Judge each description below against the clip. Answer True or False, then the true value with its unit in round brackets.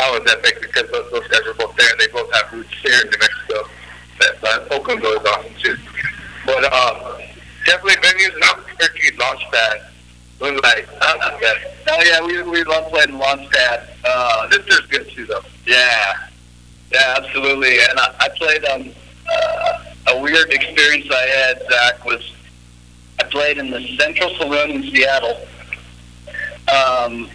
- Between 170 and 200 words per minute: False (155 wpm)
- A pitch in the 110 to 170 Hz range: True (135 Hz)